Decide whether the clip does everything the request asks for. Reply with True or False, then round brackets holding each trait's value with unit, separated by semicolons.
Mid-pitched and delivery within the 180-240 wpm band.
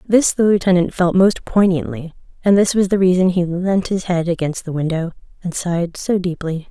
True (180 Hz; 195 wpm)